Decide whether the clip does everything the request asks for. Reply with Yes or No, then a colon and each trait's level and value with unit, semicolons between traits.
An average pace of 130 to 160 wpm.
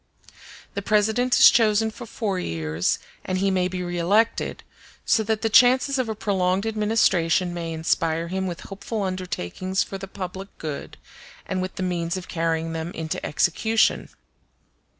Yes: average, 155 wpm